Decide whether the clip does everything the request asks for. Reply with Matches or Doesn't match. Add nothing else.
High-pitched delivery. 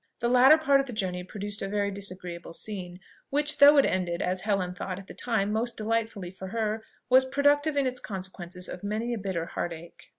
Matches